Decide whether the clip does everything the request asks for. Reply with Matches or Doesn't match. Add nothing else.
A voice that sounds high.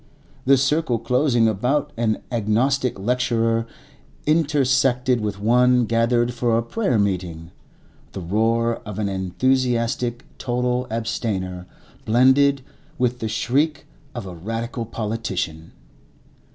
Doesn't match